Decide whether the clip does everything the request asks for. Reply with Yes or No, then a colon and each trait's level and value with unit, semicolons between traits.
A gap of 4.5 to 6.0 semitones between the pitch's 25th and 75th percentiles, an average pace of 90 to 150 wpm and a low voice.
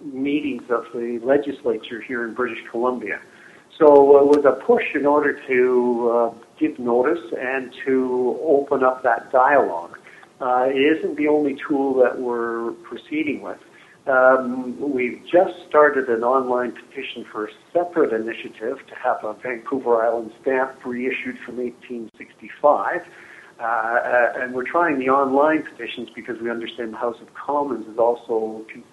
No: average, 3.0 semitones; average, 145 wpm; low, 125 Hz